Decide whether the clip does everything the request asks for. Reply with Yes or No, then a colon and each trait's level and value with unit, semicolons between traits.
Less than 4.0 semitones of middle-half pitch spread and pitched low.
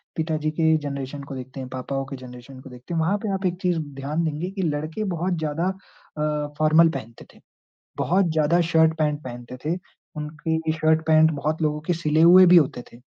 No: average, 2.7 semitones; medium, 155 Hz